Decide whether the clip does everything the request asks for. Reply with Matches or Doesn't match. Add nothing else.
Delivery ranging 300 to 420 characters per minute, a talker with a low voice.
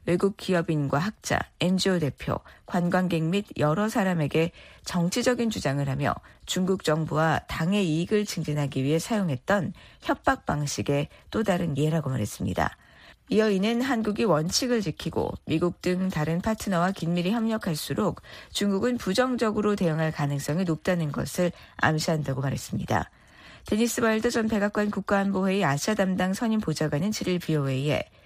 Doesn't match